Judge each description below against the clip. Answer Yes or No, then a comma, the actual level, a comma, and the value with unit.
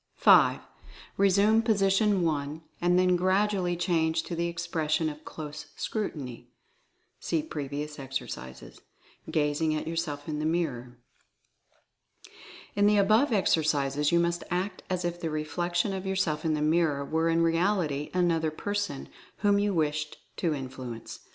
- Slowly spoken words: No, average, 145 wpm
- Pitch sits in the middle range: Yes, medium, 165 Hz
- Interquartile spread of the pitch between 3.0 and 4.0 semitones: Yes, average, 3.6 semitones